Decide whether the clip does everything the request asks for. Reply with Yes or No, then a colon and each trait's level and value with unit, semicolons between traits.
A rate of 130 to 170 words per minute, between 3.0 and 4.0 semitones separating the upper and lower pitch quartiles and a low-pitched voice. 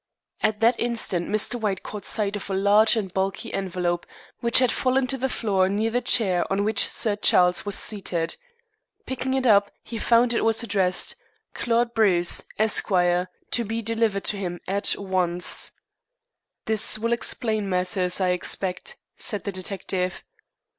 No: average, 160 wpm; average, 3.5 semitones; high, 205 Hz